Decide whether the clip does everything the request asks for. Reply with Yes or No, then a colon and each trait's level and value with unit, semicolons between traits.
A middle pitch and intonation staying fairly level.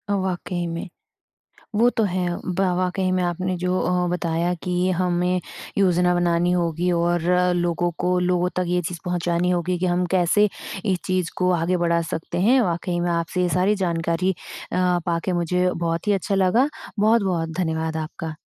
Yes: medium, 180 Hz; narrow, 1.1 semitones